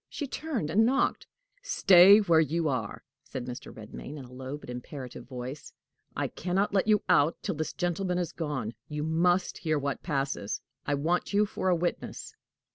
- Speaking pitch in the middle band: Yes, medium, 160 Hz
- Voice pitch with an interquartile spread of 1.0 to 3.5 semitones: No, average, 5.1 semitones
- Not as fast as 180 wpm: No, average, 185 wpm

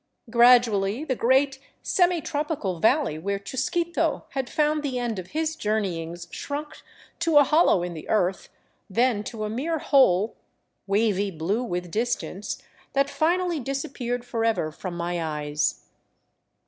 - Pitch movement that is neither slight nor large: No, wide, 7.0 semitones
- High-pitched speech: Yes, high, 235 Hz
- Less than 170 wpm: Yes, average, 140 wpm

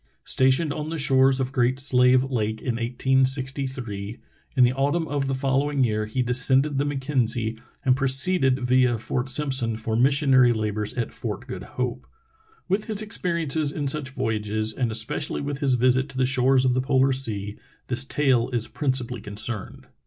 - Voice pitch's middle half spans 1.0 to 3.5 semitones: Yes, narrow, 2.4 semitones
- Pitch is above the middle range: No, low, 130 Hz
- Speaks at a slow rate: No, average, 175 wpm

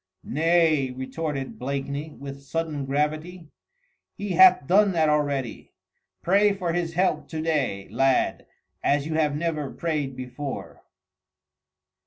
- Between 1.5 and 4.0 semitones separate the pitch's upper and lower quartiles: Yes, average, 3.2 semitones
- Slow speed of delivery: Yes, slow, 120 wpm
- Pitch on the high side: No, medium, 150 Hz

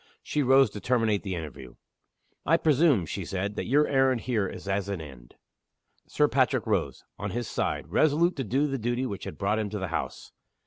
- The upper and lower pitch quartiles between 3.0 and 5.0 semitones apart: No, wide, 5.5 semitones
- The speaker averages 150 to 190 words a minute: No, average, 200 wpm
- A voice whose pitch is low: Yes, low, 110 Hz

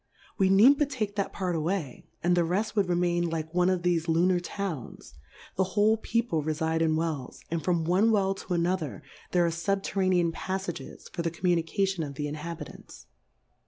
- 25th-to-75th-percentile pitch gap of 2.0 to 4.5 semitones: Yes, average, 2.9 semitones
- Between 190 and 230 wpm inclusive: No, average, 180 wpm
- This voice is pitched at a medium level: Yes, medium, 175 Hz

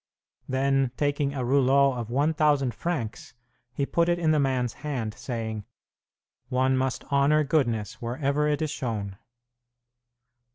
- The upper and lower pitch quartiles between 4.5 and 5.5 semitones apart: No, average, 3.3 semitones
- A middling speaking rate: No, slow, 130 wpm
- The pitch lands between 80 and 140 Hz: Yes, low, 135 Hz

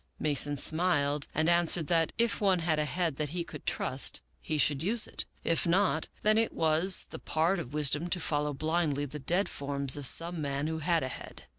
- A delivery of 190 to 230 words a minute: Yes, fast, 205 wpm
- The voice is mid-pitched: Yes, medium, 160 Hz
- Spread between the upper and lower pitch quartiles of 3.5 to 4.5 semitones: No, average, 3.1 semitones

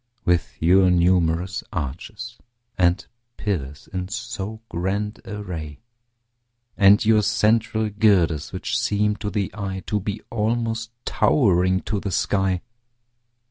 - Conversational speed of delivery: No, slow, 115 wpm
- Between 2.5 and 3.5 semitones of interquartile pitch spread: Yes, average, 3.2 semitones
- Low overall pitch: Yes, low, 100 Hz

